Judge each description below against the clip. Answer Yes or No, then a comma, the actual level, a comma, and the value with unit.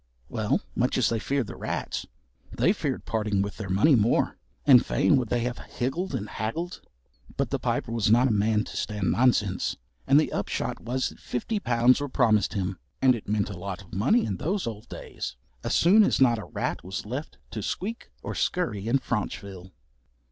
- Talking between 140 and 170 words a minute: No, average, 200 wpm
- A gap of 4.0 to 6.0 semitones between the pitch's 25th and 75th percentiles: Yes, average, 4.3 semitones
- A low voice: Yes, low, 115 Hz